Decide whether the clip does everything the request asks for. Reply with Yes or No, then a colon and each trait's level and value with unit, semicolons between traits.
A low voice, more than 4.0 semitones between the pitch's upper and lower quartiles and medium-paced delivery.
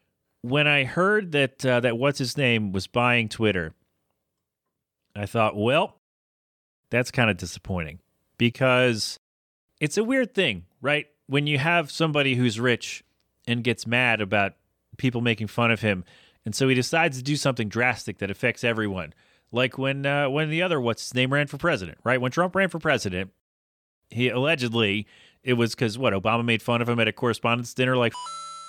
Yes: low, 120 Hz; average, 4.5 semitones; average, 180 wpm